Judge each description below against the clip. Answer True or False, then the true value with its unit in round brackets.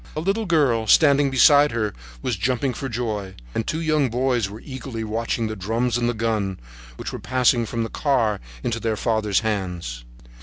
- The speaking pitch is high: False (115 Hz)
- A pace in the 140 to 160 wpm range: False (185 wpm)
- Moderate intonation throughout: True (3.6 semitones)